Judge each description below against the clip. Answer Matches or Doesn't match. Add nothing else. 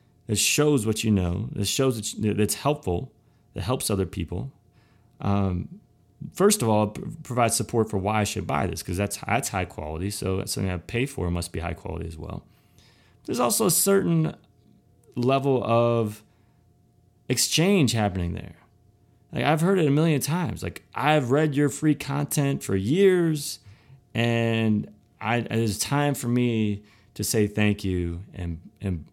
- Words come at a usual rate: Matches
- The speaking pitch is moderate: Doesn't match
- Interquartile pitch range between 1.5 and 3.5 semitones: Doesn't match